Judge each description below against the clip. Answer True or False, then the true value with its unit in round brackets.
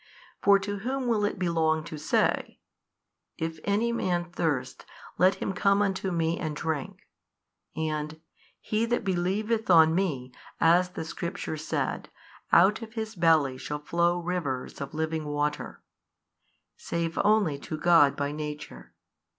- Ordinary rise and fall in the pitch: True (4.2 semitones)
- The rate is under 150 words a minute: True (140 wpm)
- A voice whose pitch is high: False (170 Hz)